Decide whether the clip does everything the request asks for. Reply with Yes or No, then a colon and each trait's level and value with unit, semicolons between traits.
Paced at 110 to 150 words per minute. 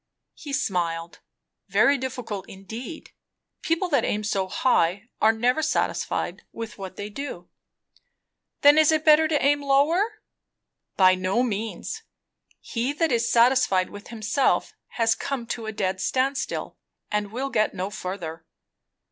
Yes: average, 140 wpm